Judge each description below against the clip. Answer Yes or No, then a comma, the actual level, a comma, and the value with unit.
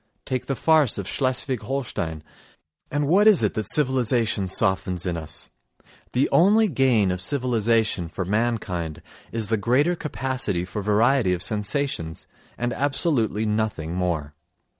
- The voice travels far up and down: Yes, wide, 6.2 semitones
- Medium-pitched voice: No, low, 115 Hz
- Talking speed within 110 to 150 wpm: Yes, slow, 135 wpm